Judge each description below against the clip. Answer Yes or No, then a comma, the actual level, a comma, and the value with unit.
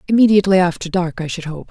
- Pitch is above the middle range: No, medium, 180 Hz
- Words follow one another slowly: No, fast, 210 wpm